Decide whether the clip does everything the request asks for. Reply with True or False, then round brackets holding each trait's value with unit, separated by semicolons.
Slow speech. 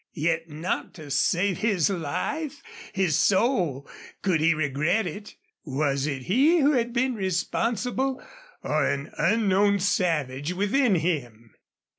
True (125 wpm)